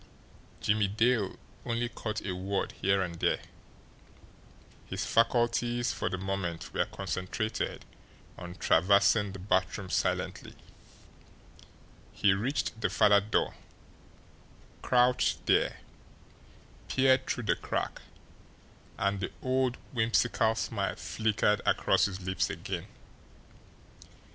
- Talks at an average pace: No, slow, 105 wpm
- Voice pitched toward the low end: Yes, low, 105 Hz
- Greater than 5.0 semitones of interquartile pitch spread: No, average, 3.5 semitones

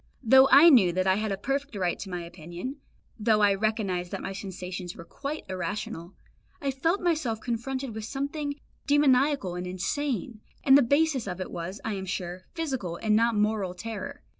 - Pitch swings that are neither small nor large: No, wide, 6.6 semitones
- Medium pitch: No, high, 215 Hz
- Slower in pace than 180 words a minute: No, average, 185 wpm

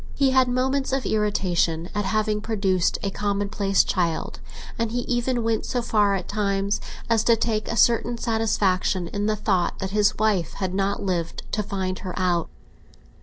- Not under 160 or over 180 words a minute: Yes, average, 170 wpm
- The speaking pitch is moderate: No, high, 205 Hz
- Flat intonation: No, average, 3.1 semitones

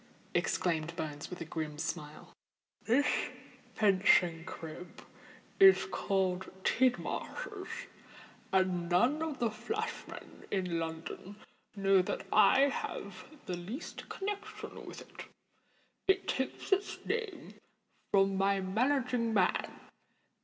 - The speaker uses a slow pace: Yes, slow, 105 wpm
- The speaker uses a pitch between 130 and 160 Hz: No, high, 195 Hz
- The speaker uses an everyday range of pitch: No, wide, 8.1 semitones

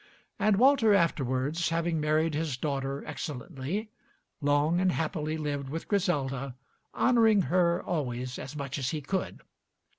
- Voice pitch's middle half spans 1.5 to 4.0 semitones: No, average, 4.4 semitones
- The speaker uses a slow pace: Yes, slow, 130 wpm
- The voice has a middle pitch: Yes, medium, 155 Hz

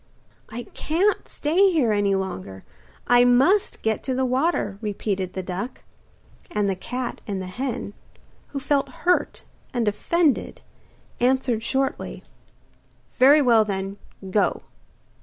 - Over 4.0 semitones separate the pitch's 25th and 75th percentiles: Yes, wide, 5.4 semitones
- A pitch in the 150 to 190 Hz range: No, high, 240 Hz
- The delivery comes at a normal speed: No, slow, 125 wpm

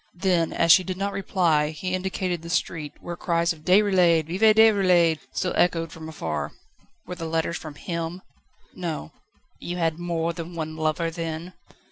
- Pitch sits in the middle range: Yes, medium, 170 Hz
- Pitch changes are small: Yes, narrow, 2.1 semitones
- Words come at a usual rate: Yes, average, 165 wpm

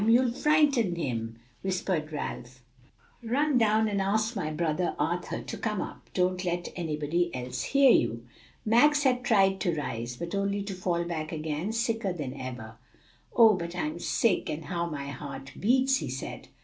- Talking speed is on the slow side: No, average, 165 wpm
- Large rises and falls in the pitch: Yes, wide, 6.6 semitones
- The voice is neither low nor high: Yes, medium, 175 Hz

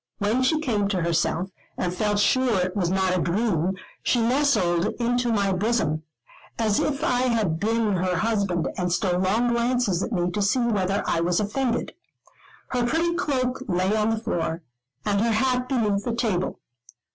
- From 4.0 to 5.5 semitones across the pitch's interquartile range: Yes, average, 4.8 semitones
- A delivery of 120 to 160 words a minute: No, average, 175 wpm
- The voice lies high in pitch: Yes, high, 210 Hz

